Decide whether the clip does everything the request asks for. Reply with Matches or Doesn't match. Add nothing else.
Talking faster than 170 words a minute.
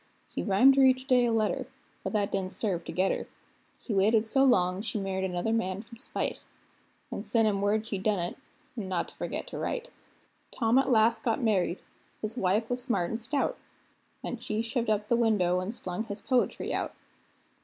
Matches